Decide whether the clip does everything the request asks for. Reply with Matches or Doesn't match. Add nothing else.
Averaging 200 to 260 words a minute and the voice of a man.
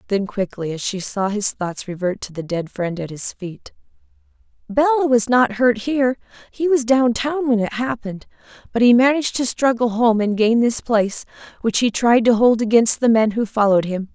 Doesn't match